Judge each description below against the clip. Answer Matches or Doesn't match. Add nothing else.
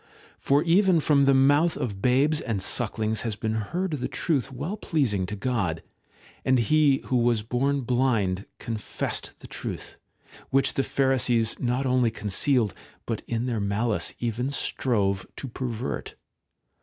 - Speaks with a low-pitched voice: Matches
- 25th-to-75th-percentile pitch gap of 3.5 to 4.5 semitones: Matches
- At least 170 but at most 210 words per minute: Doesn't match